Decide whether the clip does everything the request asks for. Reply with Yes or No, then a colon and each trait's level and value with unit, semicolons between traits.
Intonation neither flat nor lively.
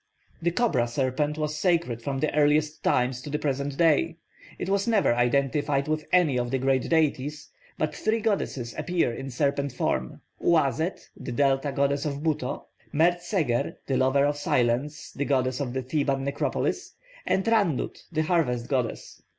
Yes: average, 3.2 semitones